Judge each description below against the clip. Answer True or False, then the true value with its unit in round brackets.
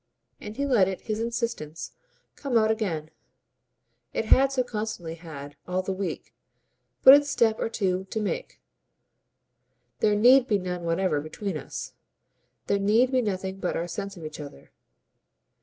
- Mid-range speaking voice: False (200 Hz)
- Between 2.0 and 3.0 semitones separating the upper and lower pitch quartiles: False (4.7 semitones)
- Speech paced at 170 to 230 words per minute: False (155 wpm)